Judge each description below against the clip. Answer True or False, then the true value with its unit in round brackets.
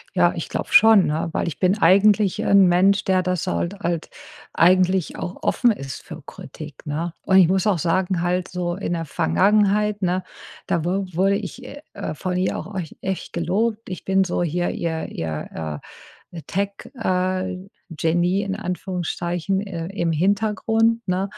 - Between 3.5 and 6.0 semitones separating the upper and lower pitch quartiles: False (2.5 semitones)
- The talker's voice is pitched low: False (185 Hz)